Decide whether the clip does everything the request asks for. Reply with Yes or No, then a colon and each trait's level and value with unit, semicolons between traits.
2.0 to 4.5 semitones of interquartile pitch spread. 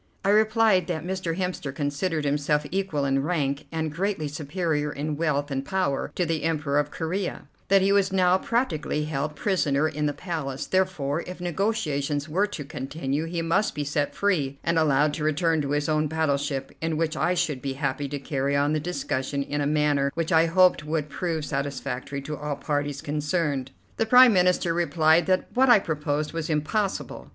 Yes: average, 3.7 semitones